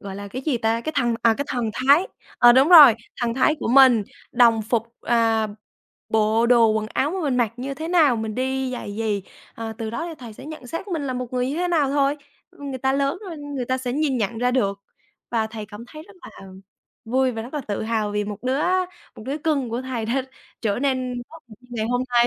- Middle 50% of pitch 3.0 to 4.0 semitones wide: Yes, average, 3.7 semitones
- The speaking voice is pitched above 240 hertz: Yes, very high, 250 Hz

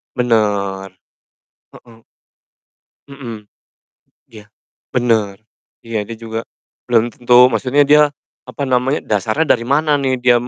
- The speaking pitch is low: Yes, low, 120 Hz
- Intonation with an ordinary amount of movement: Yes, average, 3.2 semitones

